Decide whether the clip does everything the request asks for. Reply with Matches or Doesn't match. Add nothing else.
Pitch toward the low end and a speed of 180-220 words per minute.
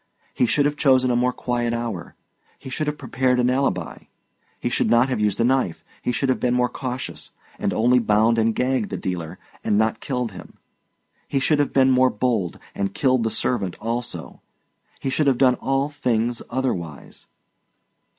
Matches